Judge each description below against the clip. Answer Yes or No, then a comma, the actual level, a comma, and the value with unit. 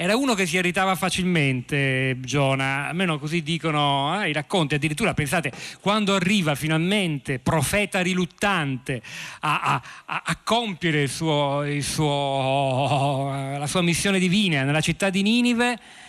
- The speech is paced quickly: No, average, 135 wpm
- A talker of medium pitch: Yes, medium, 160 Hz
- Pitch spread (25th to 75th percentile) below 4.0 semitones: No, average, 5.3 semitones